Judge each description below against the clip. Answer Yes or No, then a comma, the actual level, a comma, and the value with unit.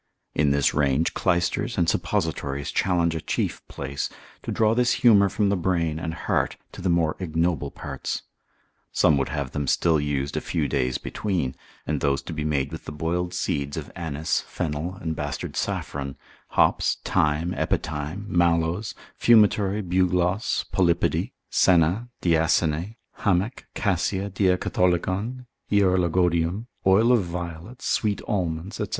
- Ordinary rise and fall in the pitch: Yes, average, 3.8 semitones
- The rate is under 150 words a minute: Yes, average, 140 wpm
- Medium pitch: No, very low, 85 Hz